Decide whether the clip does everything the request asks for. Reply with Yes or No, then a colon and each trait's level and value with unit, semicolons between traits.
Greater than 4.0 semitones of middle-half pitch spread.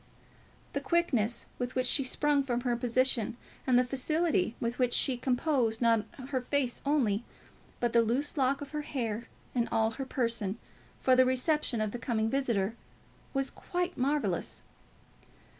No: average, 3.0 semitones